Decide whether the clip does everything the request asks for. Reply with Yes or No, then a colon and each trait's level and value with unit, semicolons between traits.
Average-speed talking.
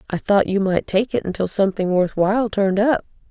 No: fast, 220 wpm